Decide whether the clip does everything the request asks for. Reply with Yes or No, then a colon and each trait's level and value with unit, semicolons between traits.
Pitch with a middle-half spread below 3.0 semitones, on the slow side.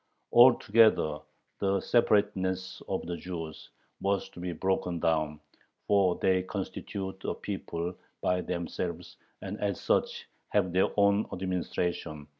Yes: narrow, 2.5 semitones; slow, 120 wpm